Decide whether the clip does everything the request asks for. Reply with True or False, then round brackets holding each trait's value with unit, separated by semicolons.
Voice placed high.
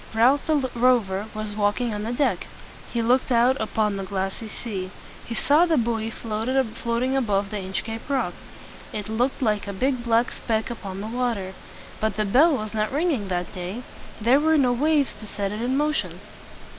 True (230 Hz)